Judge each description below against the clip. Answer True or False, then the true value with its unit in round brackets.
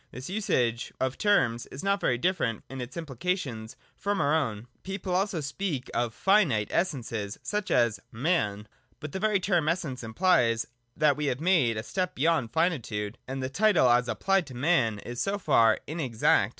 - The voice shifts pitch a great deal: True (7.6 semitones)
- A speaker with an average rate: True (180 wpm)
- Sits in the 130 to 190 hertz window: True (140 Hz)